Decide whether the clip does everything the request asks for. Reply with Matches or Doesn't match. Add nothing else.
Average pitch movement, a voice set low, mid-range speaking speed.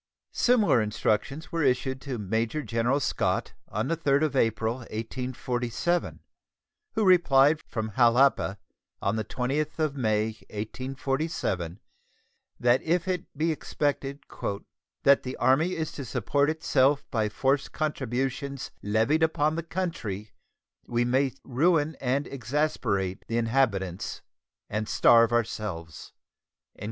Doesn't match